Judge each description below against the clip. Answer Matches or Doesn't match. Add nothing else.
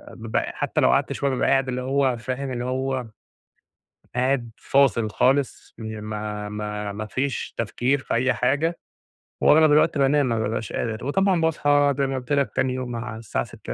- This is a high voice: Doesn't match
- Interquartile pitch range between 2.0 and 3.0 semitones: Doesn't match